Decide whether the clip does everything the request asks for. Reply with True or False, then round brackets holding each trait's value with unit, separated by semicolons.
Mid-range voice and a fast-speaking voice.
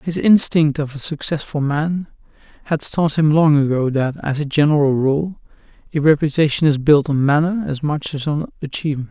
False (150 Hz; 180 wpm)